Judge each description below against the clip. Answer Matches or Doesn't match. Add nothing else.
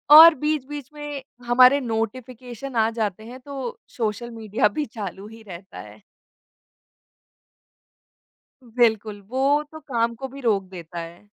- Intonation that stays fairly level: Doesn't match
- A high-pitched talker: Matches